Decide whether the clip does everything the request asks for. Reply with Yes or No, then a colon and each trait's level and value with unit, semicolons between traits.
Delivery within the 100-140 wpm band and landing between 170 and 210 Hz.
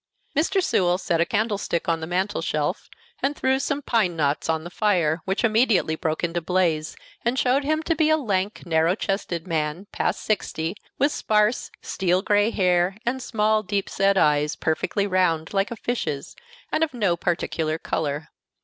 No: average, 175 wpm; high, 190 Hz